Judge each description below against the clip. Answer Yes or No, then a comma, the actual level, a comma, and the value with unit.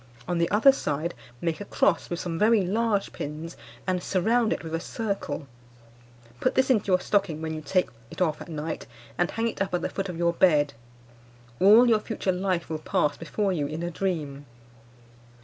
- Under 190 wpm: No, average, 200 wpm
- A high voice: No, medium, 180 Hz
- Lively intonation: No, average, 4.1 semitones